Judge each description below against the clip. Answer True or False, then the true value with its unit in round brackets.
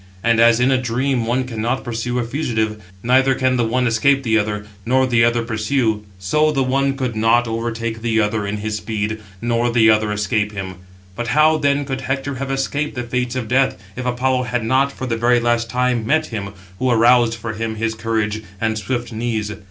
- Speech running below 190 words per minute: False (205 wpm)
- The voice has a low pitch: True (120 Hz)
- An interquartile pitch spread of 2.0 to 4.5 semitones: True (2.6 semitones)